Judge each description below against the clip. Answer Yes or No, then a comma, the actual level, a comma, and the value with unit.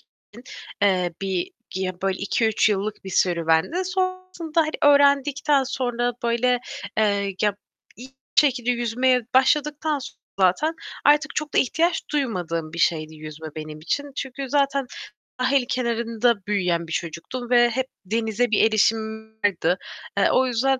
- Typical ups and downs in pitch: No, wide, 6.4 semitones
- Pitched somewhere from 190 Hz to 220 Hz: No, high, 235 Hz